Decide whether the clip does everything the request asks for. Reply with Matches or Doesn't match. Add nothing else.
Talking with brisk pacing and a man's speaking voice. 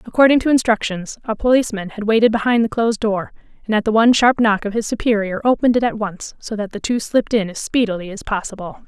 Doesn't match